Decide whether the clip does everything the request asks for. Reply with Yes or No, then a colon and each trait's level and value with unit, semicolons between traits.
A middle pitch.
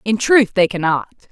No: high, 205 Hz